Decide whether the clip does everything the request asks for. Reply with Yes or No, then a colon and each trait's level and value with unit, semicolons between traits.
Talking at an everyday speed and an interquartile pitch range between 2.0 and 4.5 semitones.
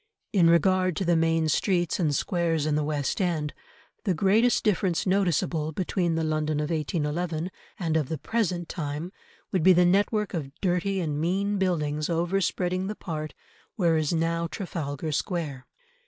Yes: average, 165 wpm; average, 3.1 semitones